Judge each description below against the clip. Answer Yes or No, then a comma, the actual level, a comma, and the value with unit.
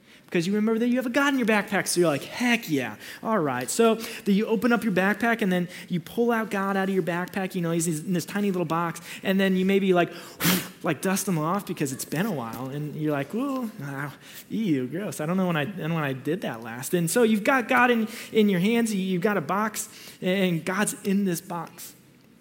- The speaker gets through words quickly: Yes, fast, 250 wpm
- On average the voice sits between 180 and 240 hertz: Yes, high, 190 Hz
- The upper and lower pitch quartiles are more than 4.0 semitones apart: Yes, average, 4.7 semitones